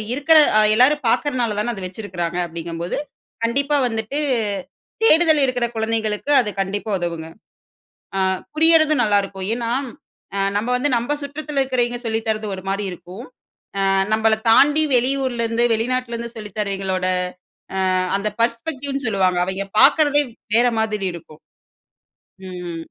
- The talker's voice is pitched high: Yes, high, 225 Hz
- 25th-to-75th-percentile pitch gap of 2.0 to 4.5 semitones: No, average, 5.1 semitones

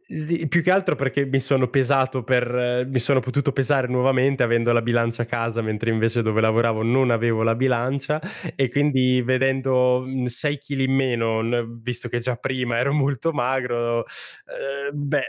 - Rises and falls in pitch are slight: Yes, narrow, 2.3 semitones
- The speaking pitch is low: Yes, low, 125 Hz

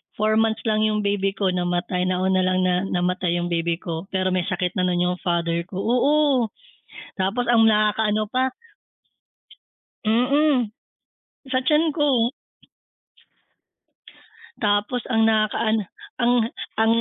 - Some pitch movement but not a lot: Yes, average, 3.9 semitones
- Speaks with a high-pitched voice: Yes, high, 210 Hz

